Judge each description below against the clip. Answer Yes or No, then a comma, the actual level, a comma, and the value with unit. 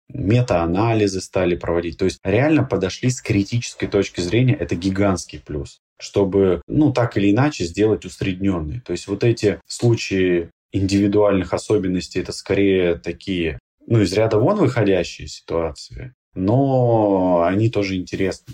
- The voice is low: Yes, low, 100 Hz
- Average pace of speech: Yes, average, 135 wpm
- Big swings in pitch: No, average, 4.0 semitones